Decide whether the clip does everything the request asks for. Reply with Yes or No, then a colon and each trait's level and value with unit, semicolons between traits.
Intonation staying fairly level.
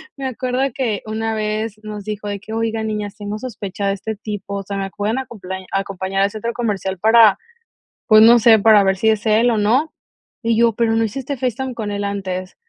Yes: narrow, 2.3 semitones